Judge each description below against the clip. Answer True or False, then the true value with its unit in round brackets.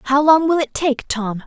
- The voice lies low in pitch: False (280 Hz)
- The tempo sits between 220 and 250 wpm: True (245 wpm)